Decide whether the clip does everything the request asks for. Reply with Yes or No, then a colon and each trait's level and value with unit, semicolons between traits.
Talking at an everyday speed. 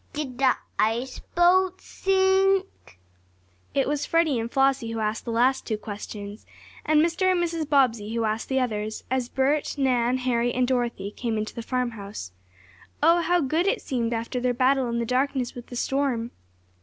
Yes: average, 175 wpm